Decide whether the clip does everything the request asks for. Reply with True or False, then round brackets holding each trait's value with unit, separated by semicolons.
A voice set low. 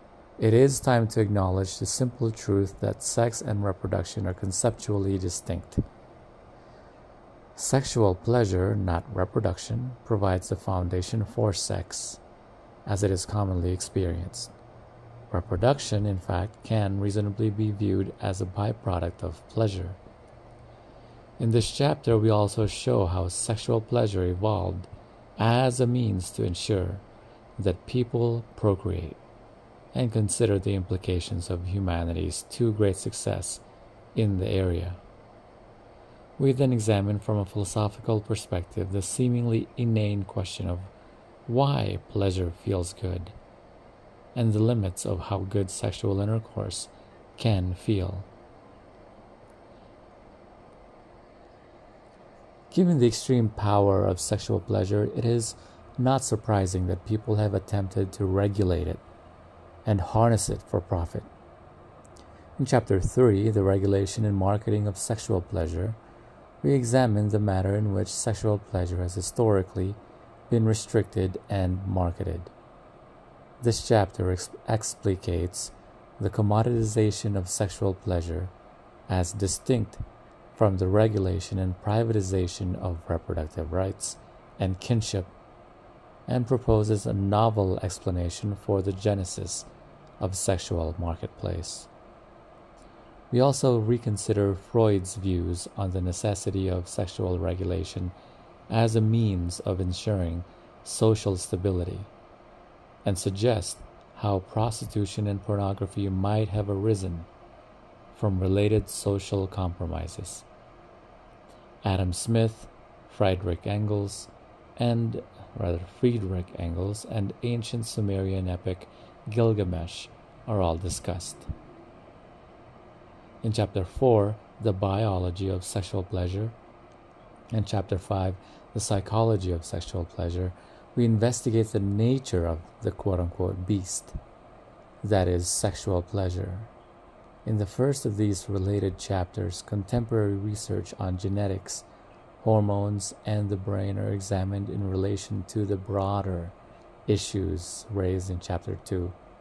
True (100 Hz)